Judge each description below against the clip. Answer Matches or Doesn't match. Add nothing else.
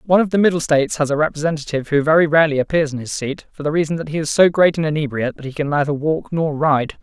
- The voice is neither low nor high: Matches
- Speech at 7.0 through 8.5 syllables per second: Matches